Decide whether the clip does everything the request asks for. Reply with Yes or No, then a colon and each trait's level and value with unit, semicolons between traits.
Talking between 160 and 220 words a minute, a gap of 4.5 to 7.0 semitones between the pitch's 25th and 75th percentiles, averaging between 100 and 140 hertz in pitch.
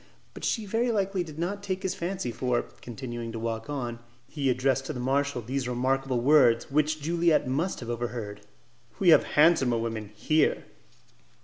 Yes: average, 170 wpm; wide, 5.6 semitones; low, 135 Hz